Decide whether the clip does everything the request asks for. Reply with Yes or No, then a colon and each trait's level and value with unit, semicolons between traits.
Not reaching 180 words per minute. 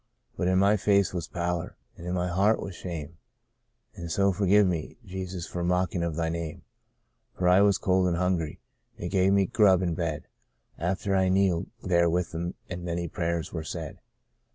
No: average, 195 wpm